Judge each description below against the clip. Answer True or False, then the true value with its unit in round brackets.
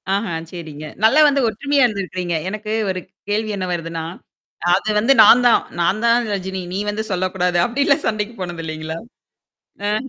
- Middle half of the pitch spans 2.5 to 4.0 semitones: False (4.4 semitones)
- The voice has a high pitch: True (200 Hz)